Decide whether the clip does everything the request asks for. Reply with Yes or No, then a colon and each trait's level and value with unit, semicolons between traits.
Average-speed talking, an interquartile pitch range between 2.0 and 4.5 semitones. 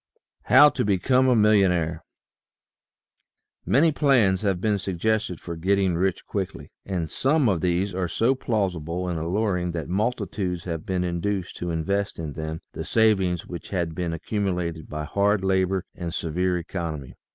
Yes: average, 155 wpm; average, 3.3 semitones